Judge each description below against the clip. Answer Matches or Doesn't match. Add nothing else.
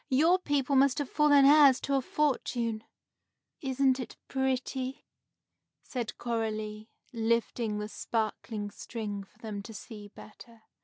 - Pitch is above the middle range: Matches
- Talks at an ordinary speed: Doesn't match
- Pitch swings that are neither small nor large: Matches